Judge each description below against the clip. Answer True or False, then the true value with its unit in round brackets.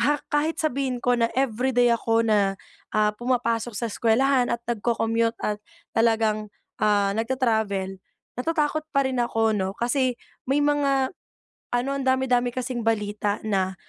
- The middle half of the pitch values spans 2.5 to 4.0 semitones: True (3.4 semitones)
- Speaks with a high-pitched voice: True (235 Hz)